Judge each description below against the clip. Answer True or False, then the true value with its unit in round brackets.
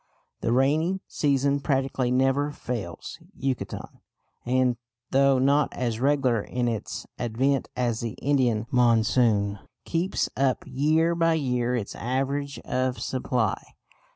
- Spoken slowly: True (120 wpm)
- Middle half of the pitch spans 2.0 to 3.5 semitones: True (2.6 semitones)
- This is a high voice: False (130 Hz)